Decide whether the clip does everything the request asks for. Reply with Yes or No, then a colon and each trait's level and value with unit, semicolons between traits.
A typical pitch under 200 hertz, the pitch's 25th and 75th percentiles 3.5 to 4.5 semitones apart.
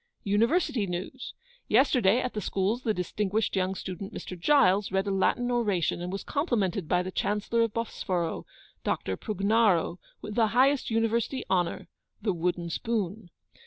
No: high, 205 Hz; average, 3.9 semitones